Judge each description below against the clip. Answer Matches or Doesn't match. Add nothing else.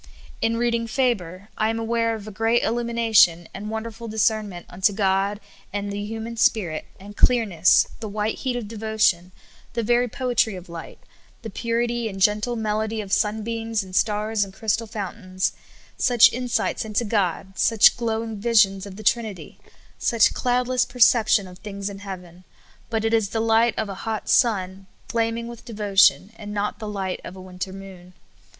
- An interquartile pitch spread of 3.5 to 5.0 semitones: Doesn't match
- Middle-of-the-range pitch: Doesn't match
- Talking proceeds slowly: Doesn't match